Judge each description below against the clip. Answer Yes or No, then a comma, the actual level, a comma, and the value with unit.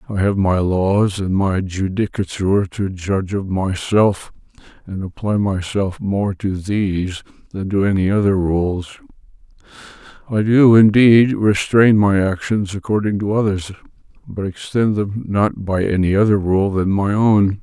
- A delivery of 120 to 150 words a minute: Yes, average, 145 wpm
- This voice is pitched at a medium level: No, low, 100 Hz